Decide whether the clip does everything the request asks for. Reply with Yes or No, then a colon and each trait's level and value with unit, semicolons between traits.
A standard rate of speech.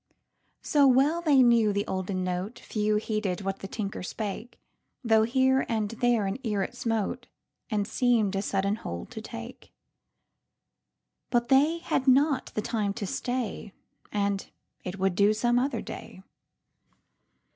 No: slow, 130 wpm